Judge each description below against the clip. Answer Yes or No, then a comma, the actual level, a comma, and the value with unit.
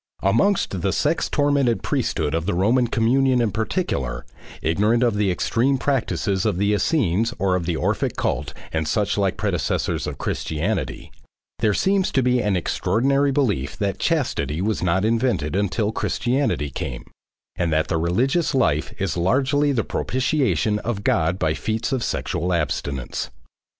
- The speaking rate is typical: Yes, average, 150 wpm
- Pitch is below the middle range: Yes, low, 105 Hz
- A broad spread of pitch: Yes, wide, 6.6 semitones